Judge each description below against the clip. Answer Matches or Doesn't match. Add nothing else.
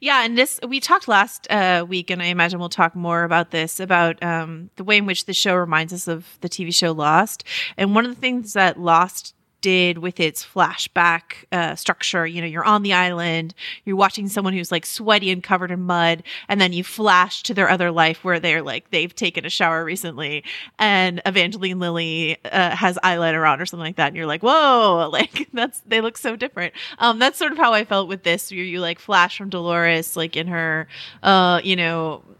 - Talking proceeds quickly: Matches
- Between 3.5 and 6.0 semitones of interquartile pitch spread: Doesn't match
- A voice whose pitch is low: Doesn't match